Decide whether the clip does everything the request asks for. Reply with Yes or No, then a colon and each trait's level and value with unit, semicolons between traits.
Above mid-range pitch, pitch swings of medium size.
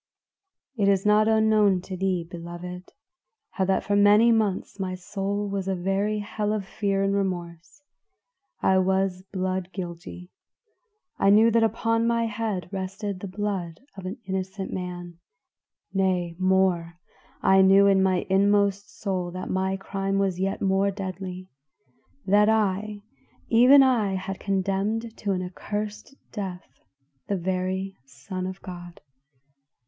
No: high, 195 Hz; narrow, 1.8 semitones